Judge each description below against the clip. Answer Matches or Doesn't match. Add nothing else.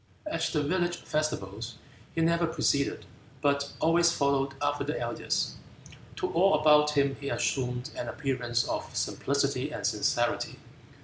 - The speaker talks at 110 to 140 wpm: Matches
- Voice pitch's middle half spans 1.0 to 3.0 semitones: Matches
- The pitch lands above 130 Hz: Matches